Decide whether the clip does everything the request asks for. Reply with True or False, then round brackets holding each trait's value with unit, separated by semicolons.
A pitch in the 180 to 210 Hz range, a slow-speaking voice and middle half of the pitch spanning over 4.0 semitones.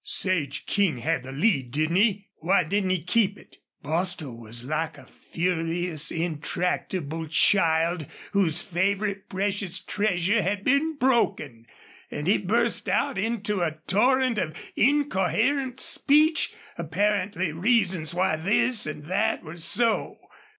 True (185 Hz; 130 wpm; 4.6 semitones)